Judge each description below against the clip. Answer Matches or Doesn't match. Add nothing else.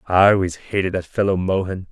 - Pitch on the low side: Matches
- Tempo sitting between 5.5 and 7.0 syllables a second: Matches